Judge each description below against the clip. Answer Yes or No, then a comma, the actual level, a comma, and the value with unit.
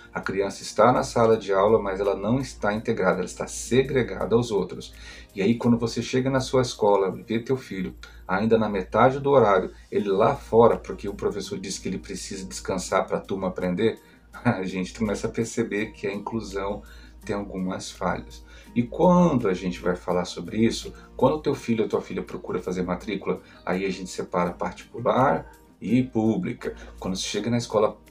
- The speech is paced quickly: Yes, fast, 190 wpm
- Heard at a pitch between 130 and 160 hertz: No, low, 105 Hz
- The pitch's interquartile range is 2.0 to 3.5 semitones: No, average, 4.3 semitones